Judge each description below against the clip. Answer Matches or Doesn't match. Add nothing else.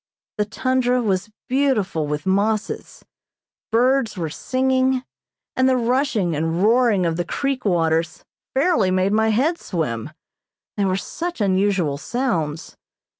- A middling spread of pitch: Doesn't match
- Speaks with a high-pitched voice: Matches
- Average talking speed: Doesn't match